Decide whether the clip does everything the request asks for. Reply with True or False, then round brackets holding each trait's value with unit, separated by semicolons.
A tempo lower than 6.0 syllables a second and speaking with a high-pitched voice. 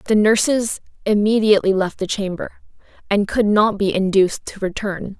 True (5.0 syllables/s; 205 Hz)